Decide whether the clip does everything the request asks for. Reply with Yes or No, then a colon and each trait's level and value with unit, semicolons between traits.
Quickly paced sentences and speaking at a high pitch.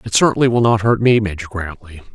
No: fast, 225 wpm; low, 105 Hz